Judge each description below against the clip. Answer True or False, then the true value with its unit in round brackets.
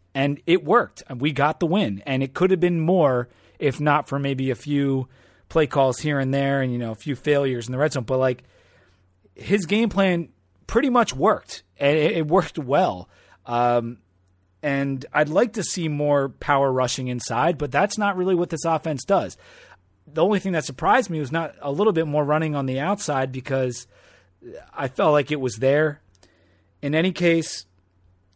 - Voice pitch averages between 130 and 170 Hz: True (140 Hz)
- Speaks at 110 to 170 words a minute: False (190 wpm)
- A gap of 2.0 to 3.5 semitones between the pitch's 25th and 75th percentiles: False (4.6 semitones)